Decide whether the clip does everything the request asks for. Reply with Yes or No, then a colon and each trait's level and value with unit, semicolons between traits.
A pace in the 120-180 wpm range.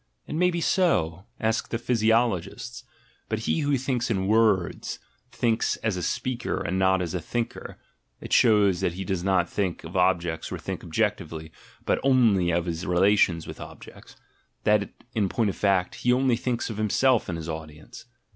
No: average, 190 wpm